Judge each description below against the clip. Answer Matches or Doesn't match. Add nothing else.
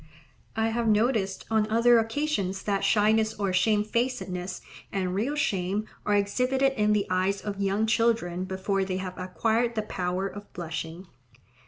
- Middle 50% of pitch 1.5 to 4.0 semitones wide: Matches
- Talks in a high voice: Matches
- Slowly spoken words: Doesn't match